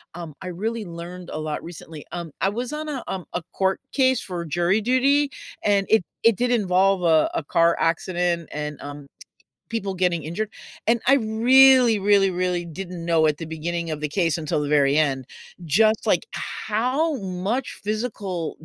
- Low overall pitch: No, medium, 180 Hz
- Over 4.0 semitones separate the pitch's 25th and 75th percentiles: Yes, average, 4.9 semitones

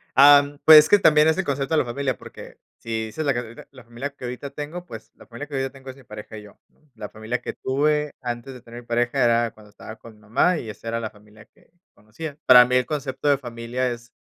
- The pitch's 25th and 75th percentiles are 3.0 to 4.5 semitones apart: Yes, average, 3.6 semitones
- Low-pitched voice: Yes, low, 125 Hz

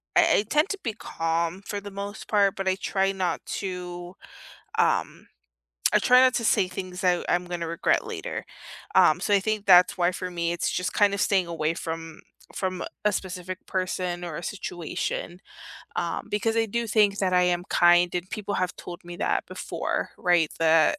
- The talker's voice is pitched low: No, medium, 185 Hz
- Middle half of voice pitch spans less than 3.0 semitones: Yes, narrow, 2.6 semitones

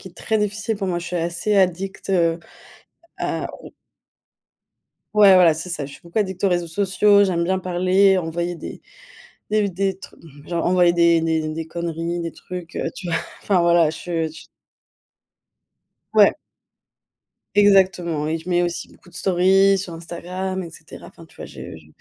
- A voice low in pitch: No, medium, 175 Hz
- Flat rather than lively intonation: Yes, narrow, 2.2 semitones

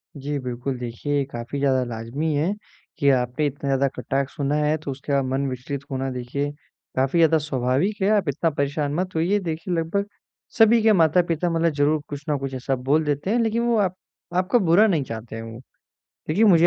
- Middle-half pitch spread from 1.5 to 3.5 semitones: No, average, 4.2 semitones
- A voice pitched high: No, medium, 145 Hz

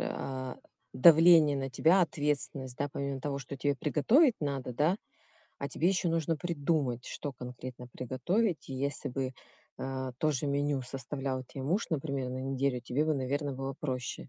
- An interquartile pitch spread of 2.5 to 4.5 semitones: Yes, average, 2.8 semitones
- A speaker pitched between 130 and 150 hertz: Yes, medium, 140 Hz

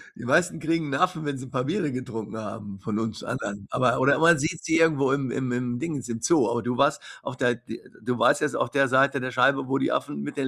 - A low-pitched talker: Yes, low, 130 Hz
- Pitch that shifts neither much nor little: Yes, average, 3.5 semitones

